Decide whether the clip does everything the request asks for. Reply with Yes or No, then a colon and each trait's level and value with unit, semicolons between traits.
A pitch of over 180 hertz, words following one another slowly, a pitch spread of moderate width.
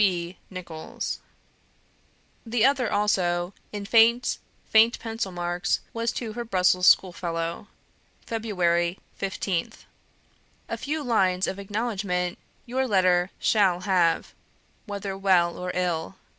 Yes: high, 190 Hz; slow, 115 wpm; average, 3.9 semitones